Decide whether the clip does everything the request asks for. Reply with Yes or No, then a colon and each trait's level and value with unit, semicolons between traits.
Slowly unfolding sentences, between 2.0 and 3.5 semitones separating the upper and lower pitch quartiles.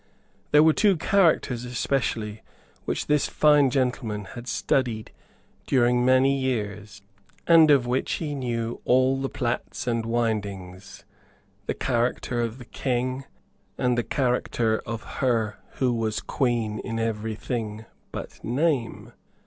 Yes: slow, 130 wpm; average, 2.9 semitones